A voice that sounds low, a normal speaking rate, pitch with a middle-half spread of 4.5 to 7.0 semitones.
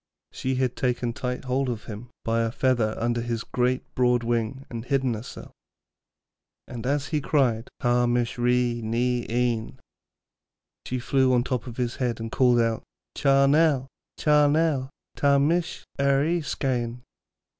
No: low, 125 Hz; average, 155 wpm; narrow, 2.5 semitones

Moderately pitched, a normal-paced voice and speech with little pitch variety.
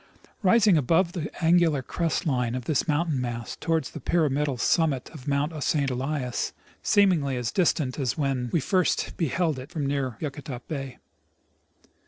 No: medium, 145 Hz; average, 160 wpm; average, 4.1 semitones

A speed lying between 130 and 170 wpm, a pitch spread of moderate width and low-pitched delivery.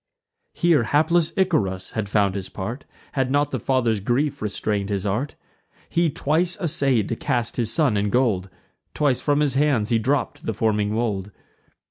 No: average, 165 wpm; wide, 5.8 semitones; low, 120 Hz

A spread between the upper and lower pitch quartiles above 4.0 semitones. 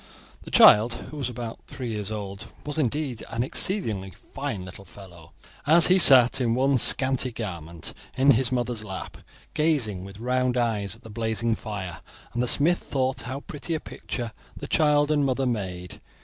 Yes: average, 4.5 semitones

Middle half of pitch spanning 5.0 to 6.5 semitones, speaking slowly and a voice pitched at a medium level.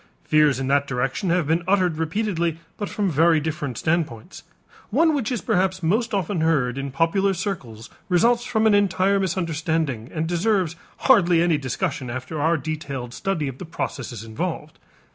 No: average, 5.3 semitones; average, 160 wpm; medium, 165 Hz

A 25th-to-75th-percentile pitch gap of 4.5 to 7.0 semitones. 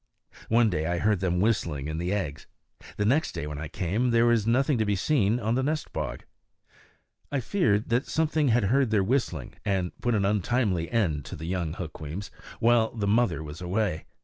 Yes: wide, 5.4 semitones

